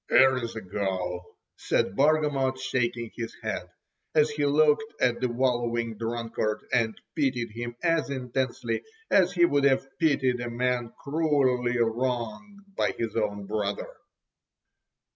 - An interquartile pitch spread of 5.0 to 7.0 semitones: No, average, 3.4 semitones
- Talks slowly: Yes, slow, 130 wpm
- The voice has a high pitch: No, low, 125 Hz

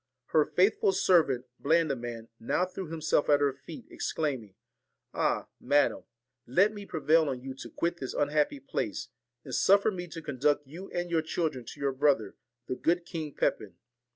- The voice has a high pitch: No, medium, 155 Hz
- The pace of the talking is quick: No, average, 170 wpm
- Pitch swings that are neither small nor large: Yes, average, 4.3 semitones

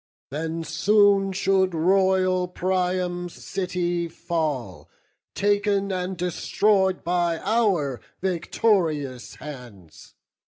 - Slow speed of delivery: Yes, slow, 80 wpm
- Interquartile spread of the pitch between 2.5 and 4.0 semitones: Yes, average, 2.9 semitones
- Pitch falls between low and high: Yes, medium, 180 Hz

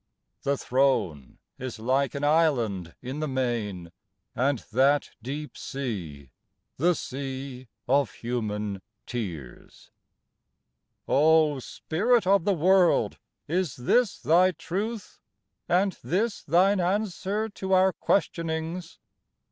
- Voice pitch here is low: No, medium, 145 Hz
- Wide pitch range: Yes, wide, 6.7 semitones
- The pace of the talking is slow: Yes, slow, 105 wpm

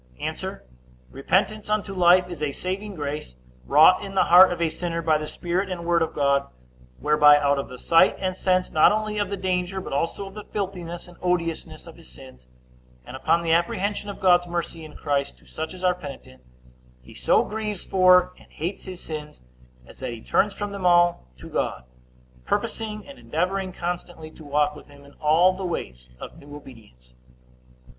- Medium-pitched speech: Yes, medium, 175 Hz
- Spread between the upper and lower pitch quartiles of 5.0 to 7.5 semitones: No, average, 4.1 semitones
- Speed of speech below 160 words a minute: No, average, 195 wpm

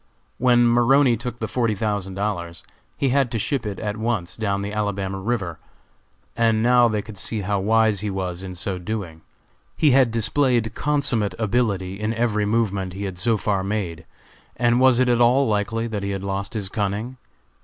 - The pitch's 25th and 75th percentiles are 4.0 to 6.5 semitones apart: No, average, 3.3 semitones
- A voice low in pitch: Yes, low, 110 Hz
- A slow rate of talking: No, average, 185 wpm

